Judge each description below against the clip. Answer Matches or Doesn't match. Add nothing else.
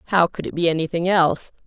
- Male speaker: Doesn't match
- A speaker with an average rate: Doesn't match